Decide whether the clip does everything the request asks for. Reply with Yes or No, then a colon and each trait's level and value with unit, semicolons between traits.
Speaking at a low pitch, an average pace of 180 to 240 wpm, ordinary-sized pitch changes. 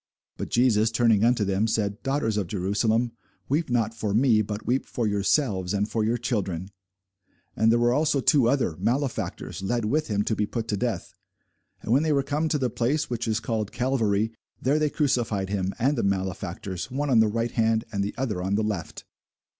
Yes: low, 115 Hz; average, 200 wpm; average, 3.6 semitones